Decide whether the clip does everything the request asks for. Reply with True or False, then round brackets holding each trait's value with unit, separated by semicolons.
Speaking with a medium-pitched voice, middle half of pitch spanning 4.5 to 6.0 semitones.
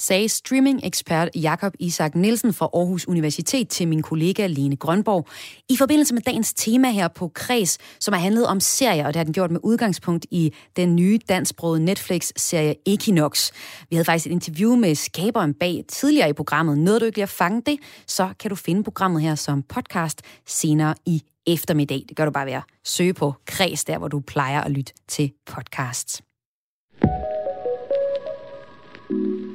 True (170 Hz; 5.4 semitones)